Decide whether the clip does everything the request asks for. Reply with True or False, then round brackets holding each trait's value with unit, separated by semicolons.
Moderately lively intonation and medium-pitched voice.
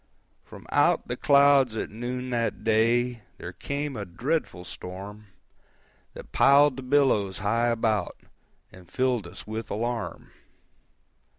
False (3.5 semitones; 120 Hz)